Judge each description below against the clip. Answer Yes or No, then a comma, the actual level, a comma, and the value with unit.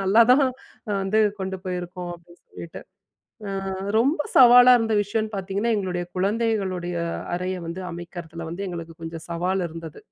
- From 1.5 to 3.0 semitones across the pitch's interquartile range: No, average, 3.8 semitones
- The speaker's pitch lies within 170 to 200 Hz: Yes, medium, 185 Hz